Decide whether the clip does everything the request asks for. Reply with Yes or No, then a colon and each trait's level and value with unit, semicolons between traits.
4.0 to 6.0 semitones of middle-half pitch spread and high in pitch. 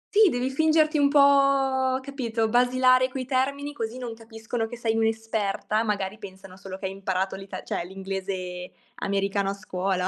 Yes: average, 5.1 semitones; high, 225 Hz